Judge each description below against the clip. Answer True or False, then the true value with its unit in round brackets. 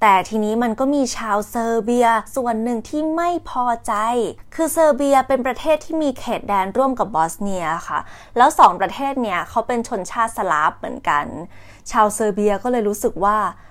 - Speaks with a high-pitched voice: True (230 Hz)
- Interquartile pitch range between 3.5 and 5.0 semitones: True (3.9 semitones)